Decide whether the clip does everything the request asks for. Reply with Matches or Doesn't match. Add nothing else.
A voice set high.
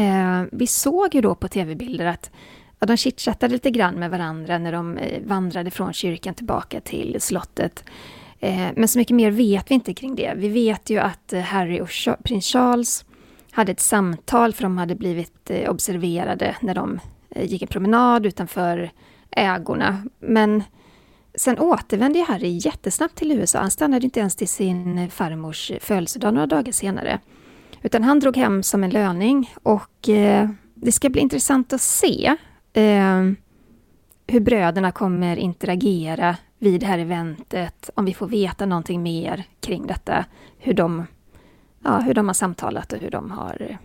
Matches